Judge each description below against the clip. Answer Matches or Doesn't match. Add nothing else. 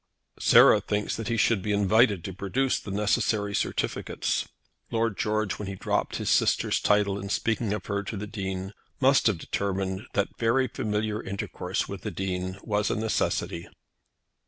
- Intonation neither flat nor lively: Doesn't match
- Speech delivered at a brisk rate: Doesn't match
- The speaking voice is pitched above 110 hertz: Doesn't match